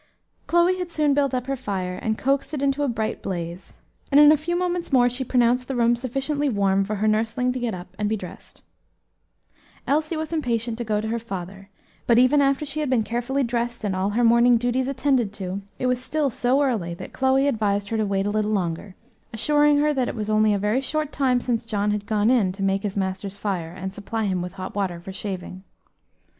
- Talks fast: Yes, fast, 225 wpm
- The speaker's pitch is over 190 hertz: Yes, high, 230 Hz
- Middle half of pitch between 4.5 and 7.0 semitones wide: Yes, average, 5.1 semitones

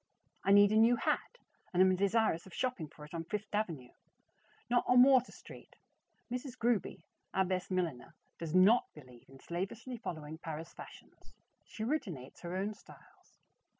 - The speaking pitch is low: No, high, 190 Hz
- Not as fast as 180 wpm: Yes, average, 160 wpm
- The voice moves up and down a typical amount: No, wide, 5.7 semitones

